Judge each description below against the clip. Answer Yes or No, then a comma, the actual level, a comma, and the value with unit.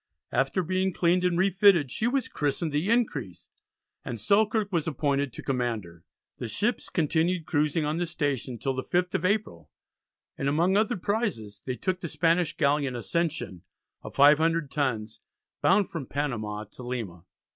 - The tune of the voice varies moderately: No, wide, 6.0 semitones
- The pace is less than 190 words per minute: Yes, average, 160 wpm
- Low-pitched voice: No, medium, 150 Hz